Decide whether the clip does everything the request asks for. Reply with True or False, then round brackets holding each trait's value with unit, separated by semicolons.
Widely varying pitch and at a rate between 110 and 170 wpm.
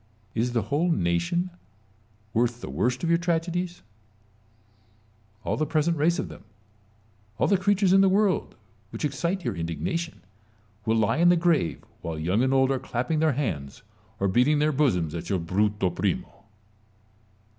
True (8.6 semitones; 160 wpm)